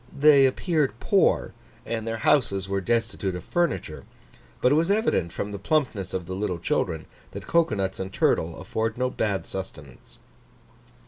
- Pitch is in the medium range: No, low, 110 Hz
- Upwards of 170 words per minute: No, average, 165 wpm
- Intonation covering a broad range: Yes, wide, 6.3 semitones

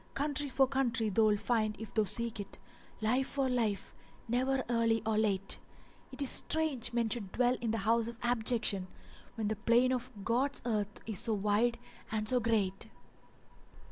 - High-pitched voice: Yes, high, 230 Hz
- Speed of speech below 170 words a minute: No, average, 175 wpm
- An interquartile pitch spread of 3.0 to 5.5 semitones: No, narrow, 2.6 semitones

